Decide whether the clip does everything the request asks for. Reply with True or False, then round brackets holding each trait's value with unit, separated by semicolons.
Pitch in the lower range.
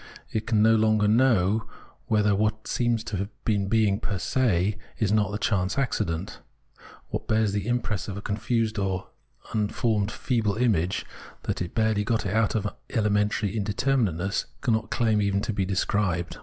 True (105 Hz)